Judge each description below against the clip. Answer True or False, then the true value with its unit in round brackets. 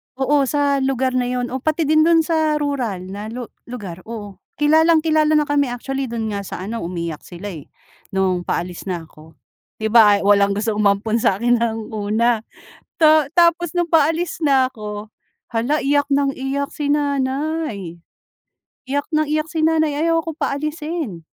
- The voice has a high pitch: True (265 Hz)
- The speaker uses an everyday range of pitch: False (6.6 semitones)